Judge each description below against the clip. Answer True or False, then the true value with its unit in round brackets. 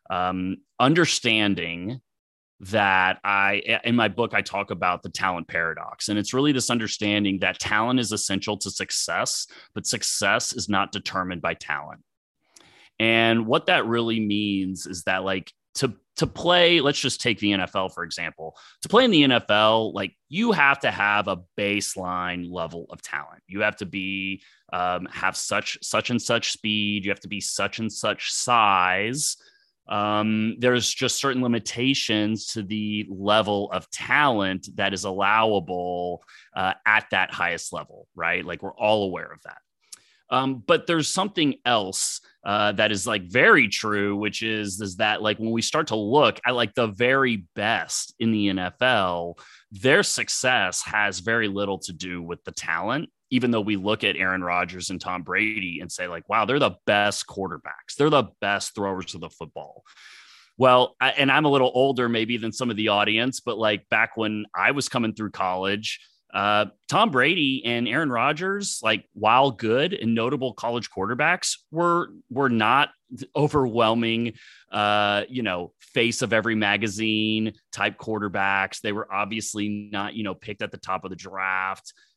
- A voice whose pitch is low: True (105 Hz)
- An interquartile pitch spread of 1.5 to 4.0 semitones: True (3.4 semitones)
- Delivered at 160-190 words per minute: True (170 wpm)